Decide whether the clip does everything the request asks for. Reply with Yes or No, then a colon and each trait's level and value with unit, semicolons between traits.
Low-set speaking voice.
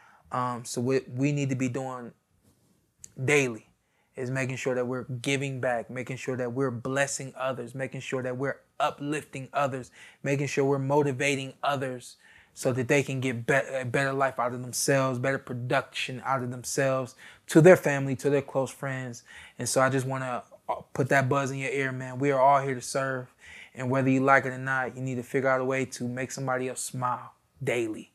Yes: low, 130 Hz